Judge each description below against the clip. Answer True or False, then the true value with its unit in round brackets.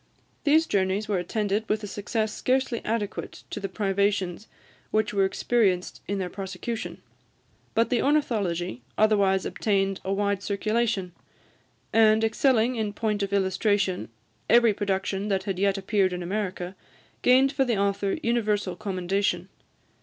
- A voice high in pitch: True (205 Hz)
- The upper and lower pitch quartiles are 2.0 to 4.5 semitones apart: True (2.5 semitones)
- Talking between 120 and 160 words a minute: True (140 wpm)